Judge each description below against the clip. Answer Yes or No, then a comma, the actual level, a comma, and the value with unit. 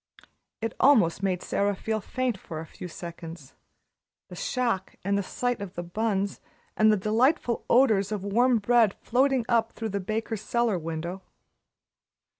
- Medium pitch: No, high, 215 Hz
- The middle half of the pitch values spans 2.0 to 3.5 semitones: No, average, 4.0 semitones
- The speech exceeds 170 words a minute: No, average, 155 wpm